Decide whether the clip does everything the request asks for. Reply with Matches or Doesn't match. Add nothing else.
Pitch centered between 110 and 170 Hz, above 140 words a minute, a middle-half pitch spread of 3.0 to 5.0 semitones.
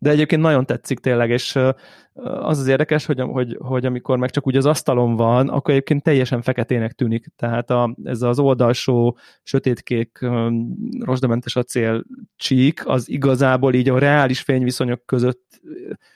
Doesn't match